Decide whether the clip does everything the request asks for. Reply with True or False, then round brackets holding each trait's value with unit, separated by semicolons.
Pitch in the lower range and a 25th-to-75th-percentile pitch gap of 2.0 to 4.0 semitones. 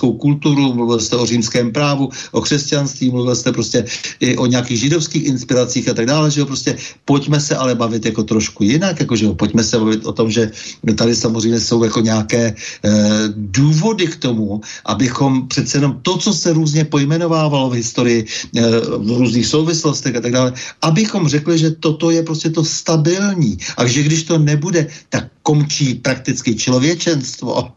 False (130 Hz; 4.7 semitones)